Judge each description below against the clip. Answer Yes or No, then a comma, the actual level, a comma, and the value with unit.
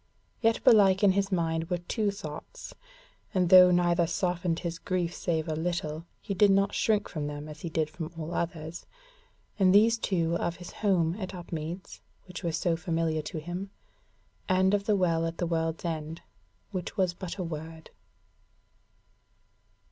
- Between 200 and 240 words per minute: No, average, 170 wpm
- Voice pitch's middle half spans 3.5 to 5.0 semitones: No, narrow, 2.5 semitones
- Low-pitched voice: No, medium, 175 Hz